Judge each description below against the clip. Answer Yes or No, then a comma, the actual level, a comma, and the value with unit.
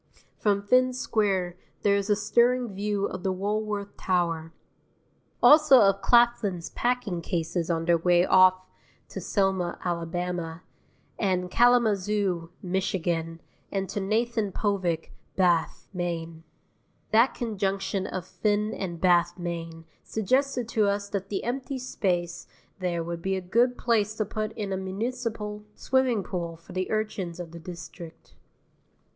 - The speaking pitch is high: Yes, high, 195 Hz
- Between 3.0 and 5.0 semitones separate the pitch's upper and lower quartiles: Yes, average, 3.6 semitones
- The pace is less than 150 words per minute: Yes, slow, 135 wpm